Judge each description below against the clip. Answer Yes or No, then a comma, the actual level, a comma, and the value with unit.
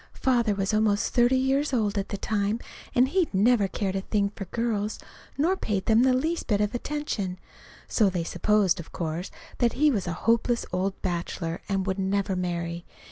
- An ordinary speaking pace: Yes, average, 190 wpm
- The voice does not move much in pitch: No, average, 4.1 semitones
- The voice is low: No, high, 205 Hz